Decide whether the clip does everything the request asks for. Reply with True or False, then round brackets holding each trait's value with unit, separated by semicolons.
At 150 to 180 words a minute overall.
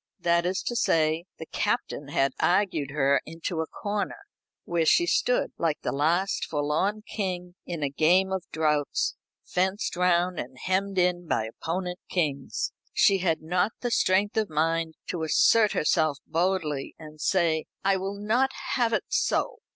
True (160 wpm)